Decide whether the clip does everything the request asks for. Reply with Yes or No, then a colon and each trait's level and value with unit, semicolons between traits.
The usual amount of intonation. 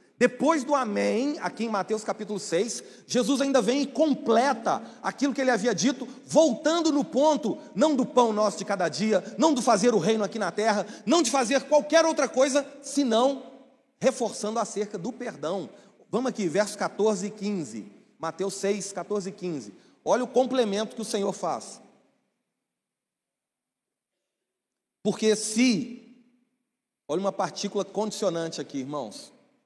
Yes: average, 4.5 semitones